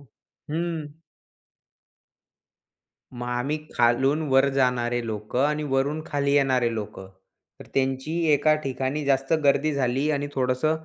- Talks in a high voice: No, low, 135 Hz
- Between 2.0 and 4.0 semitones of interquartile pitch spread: Yes, average, 2.8 semitones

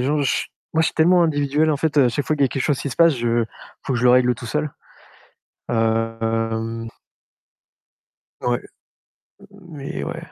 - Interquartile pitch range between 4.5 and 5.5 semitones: Yes, average, 4.8 semitones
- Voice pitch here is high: No, low, 135 Hz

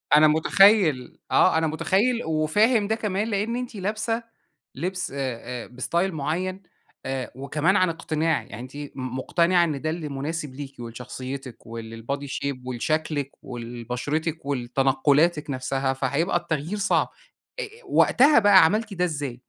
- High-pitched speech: No, medium, 155 Hz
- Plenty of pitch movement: Yes, wide, 5.8 semitones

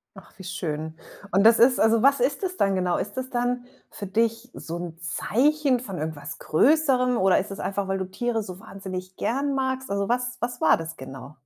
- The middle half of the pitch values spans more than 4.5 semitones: Yes, wide, 5.4 semitones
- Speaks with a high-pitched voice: Yes, high, 210 Hz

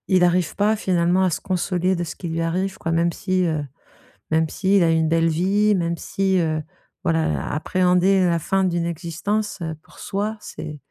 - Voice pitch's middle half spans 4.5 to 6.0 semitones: No, narrow, 2.4 semitones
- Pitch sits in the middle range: Yes, medium, 180 Hz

